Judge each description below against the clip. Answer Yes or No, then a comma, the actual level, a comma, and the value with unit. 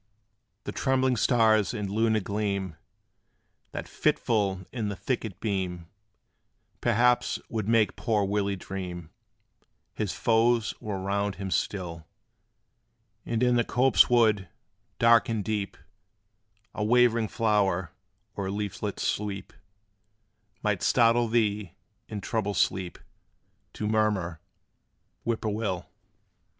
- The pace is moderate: No, slow, 110 wpm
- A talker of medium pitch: No, low, 105 Hz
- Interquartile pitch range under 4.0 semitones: Yes, average, 2.9 semitones